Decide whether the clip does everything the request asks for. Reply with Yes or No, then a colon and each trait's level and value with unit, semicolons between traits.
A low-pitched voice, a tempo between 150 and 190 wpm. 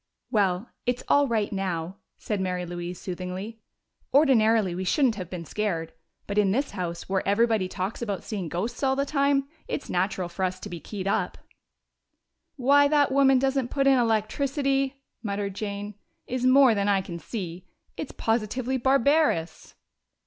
No: high, 215 Hz; average, 160 wpm